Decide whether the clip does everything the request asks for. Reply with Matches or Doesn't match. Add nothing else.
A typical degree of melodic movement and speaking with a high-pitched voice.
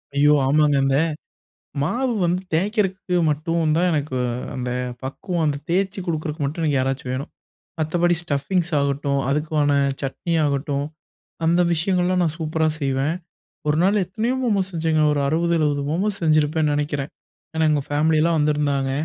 Doesn't match